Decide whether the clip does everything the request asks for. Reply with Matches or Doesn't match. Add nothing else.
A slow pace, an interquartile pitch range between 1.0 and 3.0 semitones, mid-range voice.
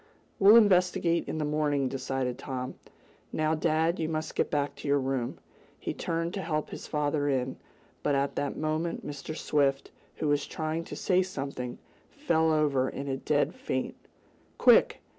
Doesn't match